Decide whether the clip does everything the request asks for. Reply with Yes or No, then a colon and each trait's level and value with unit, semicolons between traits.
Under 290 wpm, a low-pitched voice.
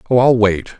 Yes: fast, 225 wpm; low, 110 Hz